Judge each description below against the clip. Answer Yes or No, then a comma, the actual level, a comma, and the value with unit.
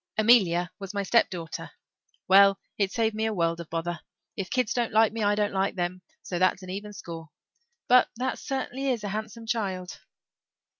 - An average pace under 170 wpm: No, average, 190 wpm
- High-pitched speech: Yes, high, 200 Hz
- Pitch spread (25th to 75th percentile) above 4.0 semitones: No, average, 3.5 semitones